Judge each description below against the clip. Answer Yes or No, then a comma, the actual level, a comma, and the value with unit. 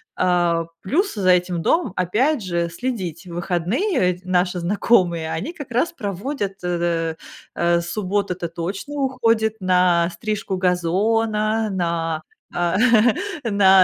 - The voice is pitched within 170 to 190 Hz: Yes, medium, 185 Hz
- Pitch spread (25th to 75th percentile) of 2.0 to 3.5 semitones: No, average, 4.1 semitones